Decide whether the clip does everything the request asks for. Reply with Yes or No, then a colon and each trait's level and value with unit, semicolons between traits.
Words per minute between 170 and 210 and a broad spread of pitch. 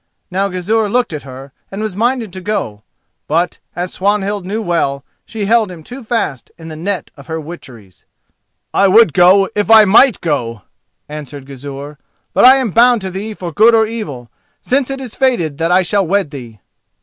Yes: average, 190 wpm; wide, 6.6 semitones